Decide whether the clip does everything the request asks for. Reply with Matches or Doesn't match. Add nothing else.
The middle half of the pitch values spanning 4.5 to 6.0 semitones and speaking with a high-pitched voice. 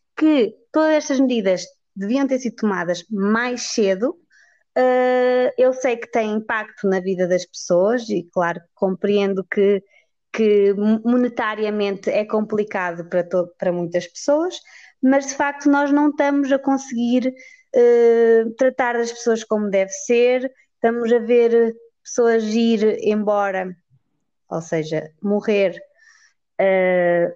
Matches